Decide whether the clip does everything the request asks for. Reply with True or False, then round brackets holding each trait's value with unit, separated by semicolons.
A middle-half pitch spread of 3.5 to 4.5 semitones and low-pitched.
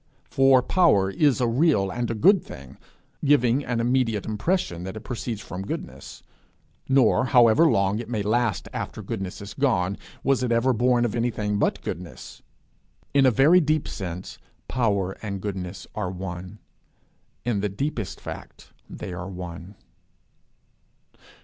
False (4.9 semitones; 110 Hz)